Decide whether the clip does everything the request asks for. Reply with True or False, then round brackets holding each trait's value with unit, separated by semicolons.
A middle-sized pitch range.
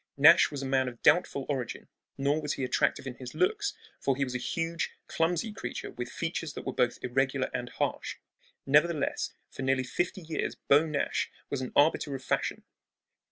True (3.8 semitones)